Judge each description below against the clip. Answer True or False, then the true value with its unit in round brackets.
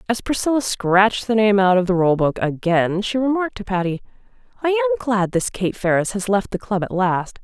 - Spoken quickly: True (220 wpm)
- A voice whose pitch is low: False (205 Hz)